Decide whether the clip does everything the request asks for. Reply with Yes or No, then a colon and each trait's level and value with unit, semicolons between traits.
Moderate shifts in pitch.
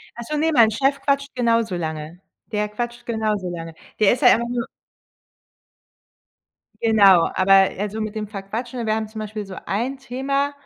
Yes: average, 3.5 semitones